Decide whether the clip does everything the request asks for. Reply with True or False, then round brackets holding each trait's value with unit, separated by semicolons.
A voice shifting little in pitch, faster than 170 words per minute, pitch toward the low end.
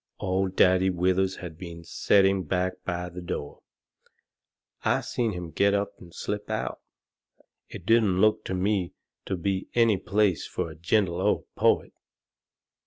False (2.2 semitones; 150 wpm; 95 Hz)